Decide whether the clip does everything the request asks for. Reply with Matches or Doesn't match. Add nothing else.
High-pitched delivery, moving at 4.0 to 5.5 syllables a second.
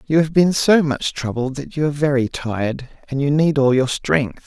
Doesn't match